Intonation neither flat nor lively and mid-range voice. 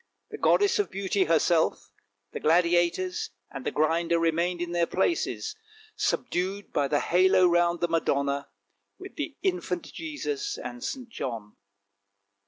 Yes: average, 3.3 semitones; medium, 175 Hz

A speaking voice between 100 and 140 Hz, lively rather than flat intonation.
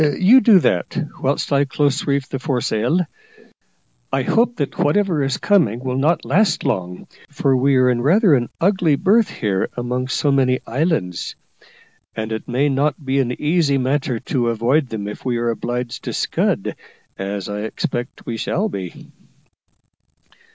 No: low, 135 Hz; average, 4.1 semitones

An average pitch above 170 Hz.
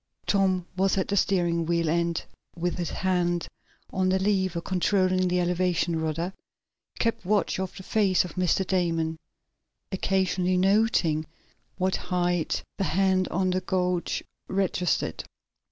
Yes: medium, 185 Hz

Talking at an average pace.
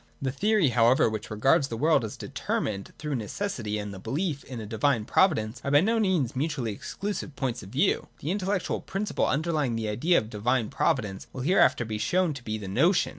No: fast, 210 wpm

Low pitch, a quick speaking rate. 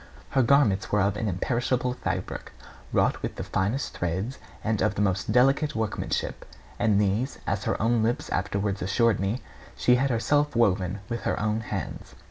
No: low, 110 Hz; average, 170 wpm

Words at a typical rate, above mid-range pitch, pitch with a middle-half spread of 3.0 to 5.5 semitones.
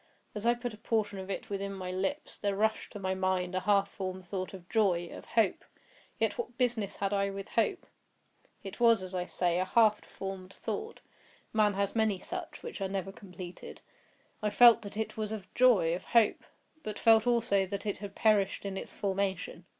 No: average, 190 wpm; high, 200 Hz; narrow, 2.6 semitones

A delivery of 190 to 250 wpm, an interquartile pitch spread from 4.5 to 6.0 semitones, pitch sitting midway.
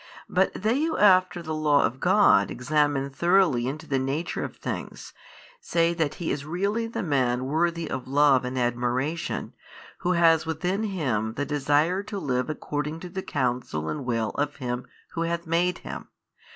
No: average, 170 wpm; average, 5.1 semitones; medium, 150 Hz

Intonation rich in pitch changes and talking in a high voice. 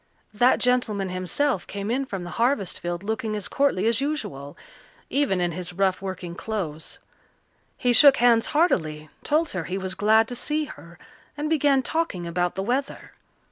Yes: wide, 6.6 semitones; high, 210 Hz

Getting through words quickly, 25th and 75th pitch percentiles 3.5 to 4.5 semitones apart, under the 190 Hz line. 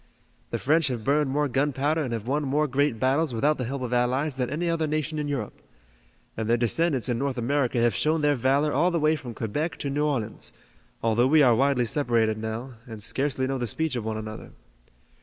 Yes: fast, 215 wpm; average, 3.8 semitones; low, 135 Hz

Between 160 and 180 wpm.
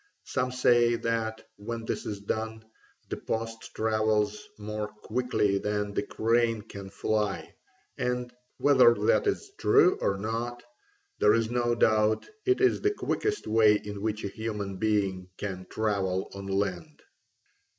No: average, 140 wpm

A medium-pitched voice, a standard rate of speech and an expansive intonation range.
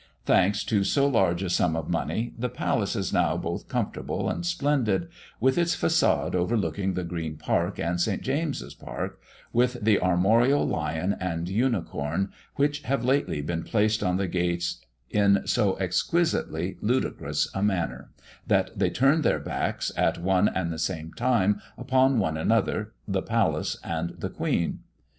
No: low, 100 Hz; average, 155 wpm; wide, 6.4 semitones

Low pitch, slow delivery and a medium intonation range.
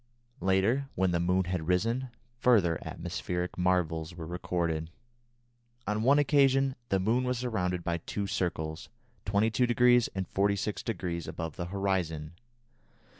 Yes: very low, 95 Hz; slow, 125 wpm; average, 4.9 semitones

